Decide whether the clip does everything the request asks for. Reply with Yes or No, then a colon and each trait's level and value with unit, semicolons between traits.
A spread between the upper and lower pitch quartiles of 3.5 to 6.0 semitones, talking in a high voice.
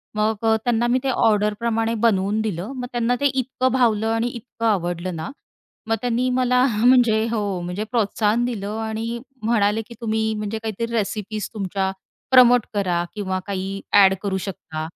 No: average, 3.0 semitones; high, 220 Hz